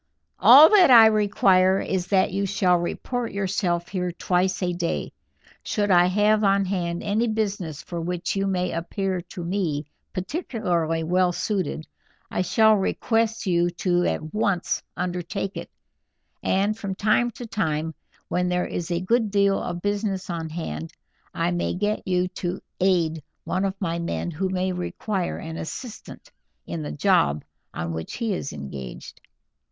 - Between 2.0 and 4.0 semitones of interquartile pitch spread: Yes, average, 2.8 semitones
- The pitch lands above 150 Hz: Yes, medium, 185 Hz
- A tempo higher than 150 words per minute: Yes, average, 160 wpm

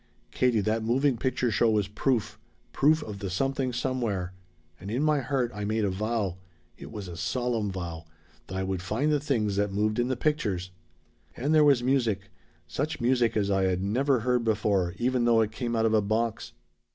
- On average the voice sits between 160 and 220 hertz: No, low, 115 Hz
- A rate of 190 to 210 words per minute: Yes, average, 200 wpm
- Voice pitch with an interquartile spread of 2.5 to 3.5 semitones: No, average, 4.2 semitones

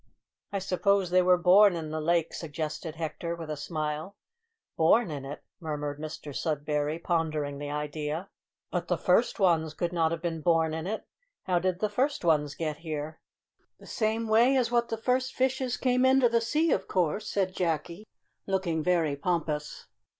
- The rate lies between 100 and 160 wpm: No, average, 175 wpm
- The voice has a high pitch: No, medium, 170 Hz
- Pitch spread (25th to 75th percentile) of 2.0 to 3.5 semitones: No, average, 4.5 semitones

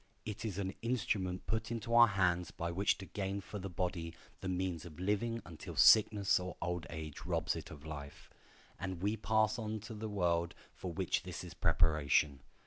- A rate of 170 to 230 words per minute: Yes, average, 195 wpm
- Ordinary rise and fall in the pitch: Yes, average, 3.9 semitones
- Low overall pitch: Yes, very low, 95 Hz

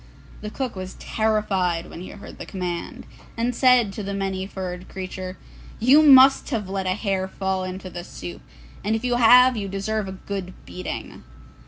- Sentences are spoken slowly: No, average, 180 wpm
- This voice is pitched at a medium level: No, high, 195 Hz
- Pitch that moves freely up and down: No, average, 3.1 semitones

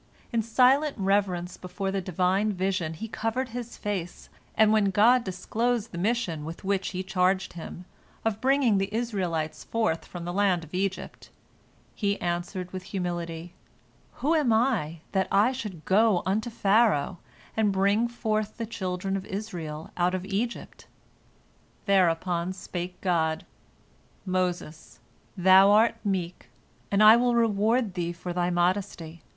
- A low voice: No, high, 195 Hz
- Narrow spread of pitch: No, average, 3.7 semitones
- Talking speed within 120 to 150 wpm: Yes, average, 145 wpm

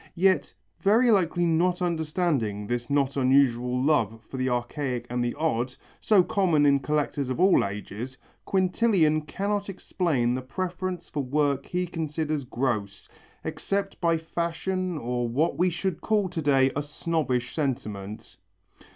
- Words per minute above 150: No, average, 140 wpm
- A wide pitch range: Yes, wide, 5.9 semitones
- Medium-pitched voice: Yes, medium, 150 Hz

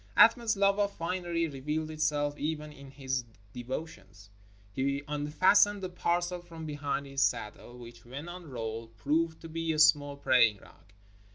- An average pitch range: Yes, average, 4.1 semitones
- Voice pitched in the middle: Yes, medium, 150 Hz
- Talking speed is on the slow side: No, average, 155 wpm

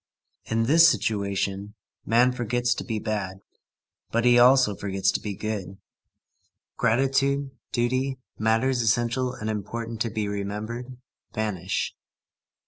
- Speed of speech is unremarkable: No, slow, 120 wpm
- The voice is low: Yes, low, 115 Hz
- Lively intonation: No, average, 3.3 semitones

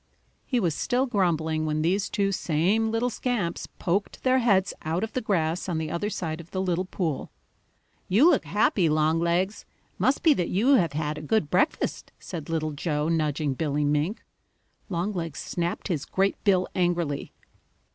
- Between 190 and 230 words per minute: No, average, 165 wpm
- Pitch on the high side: No, medium, 175 Hz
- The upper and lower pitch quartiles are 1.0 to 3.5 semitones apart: No, average, 4.4 semitones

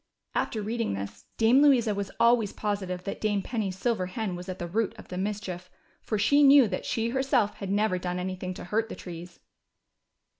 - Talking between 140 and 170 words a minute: No, average, 195 wpm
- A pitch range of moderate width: Yes, average, 3.7 semitones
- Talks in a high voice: Yes, high, 205 Hz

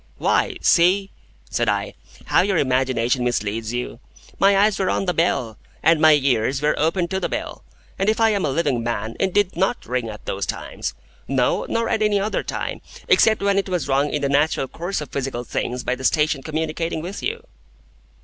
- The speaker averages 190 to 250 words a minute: Yes, average, 200 wpm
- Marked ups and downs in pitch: Yes, wide, 7.2 semitones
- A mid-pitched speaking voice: Yes, medium, 155 Hz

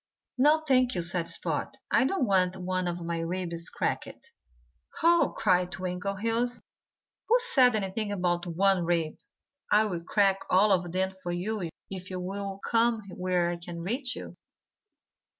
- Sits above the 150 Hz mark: Yes, high, 190 Hz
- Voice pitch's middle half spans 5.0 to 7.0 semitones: No, average, 3.8 semitones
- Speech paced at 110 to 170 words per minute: Yes, average, 145 wpm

